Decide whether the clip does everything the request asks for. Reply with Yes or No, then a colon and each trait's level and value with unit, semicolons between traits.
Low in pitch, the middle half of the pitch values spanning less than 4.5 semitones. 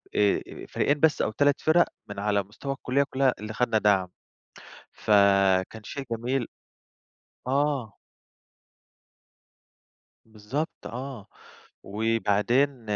No: low, 115 Hz; average, 4.8 semitones